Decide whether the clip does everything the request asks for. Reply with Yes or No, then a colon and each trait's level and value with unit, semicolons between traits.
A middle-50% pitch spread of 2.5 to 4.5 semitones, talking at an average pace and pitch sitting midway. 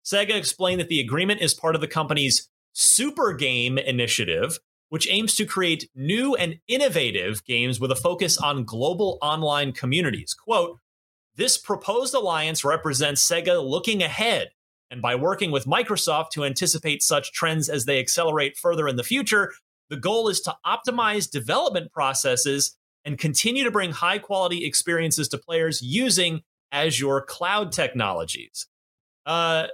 No: wide, 5.6 semitones; average, 145 wpm; medium, 160 Hz